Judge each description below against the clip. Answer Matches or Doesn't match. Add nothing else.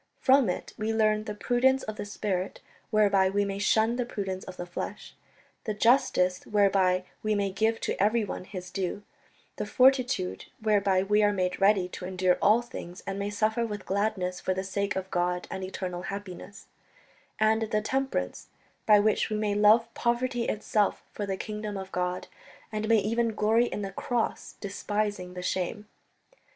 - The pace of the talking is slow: Doesn't match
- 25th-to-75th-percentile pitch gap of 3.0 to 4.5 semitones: Doesn't match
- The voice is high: Matches